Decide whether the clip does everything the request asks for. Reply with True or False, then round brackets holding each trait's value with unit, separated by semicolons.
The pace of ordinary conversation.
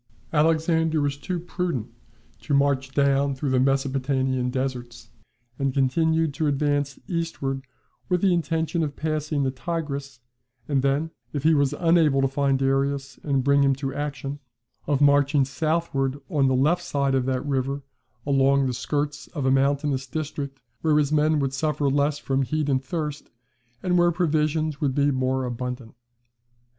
True (160 wpm)